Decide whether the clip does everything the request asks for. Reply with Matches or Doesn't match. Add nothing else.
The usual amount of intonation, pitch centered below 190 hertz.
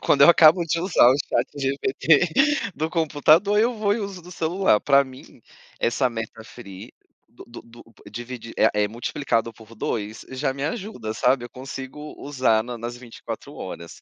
Doesn't match